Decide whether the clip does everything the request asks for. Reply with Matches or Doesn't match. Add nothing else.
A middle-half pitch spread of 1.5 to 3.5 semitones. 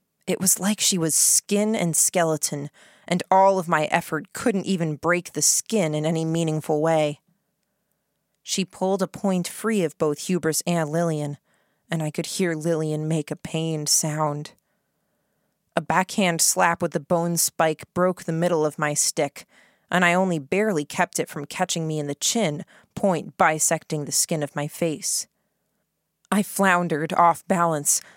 Matches